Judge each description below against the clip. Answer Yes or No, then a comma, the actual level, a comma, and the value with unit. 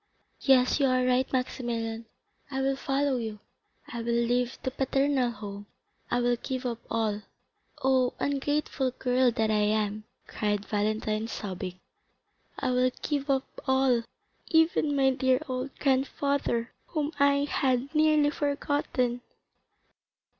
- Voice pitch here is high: Yes, very high, 255 Hz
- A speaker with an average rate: No, slow, 130 wpm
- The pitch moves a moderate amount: Yes, average, 3.0 semitones